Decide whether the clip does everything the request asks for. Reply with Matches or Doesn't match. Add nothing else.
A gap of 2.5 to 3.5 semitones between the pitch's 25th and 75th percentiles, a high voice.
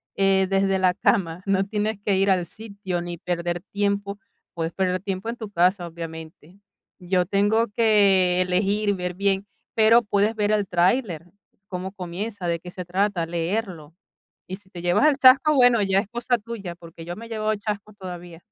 Matches